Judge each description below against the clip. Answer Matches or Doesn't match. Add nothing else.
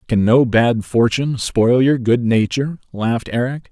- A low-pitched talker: Matches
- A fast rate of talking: Doesn't match